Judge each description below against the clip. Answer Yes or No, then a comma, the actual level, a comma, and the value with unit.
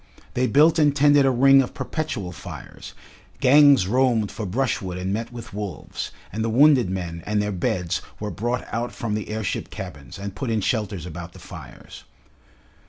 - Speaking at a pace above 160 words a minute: Yes, average, 175 wpm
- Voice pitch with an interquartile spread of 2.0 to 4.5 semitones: No, wide, 5.6 semitones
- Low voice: Yes, low, 110 Hz